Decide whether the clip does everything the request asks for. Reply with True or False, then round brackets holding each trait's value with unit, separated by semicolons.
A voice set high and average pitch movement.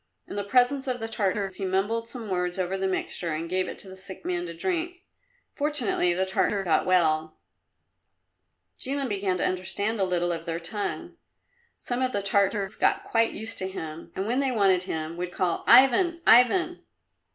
True (195 Hz; 4.9 semitones)